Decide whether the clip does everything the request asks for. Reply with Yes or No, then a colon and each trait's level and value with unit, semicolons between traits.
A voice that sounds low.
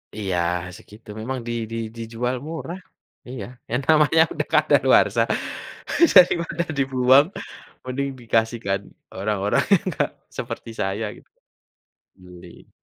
Yes: low, 120 Hz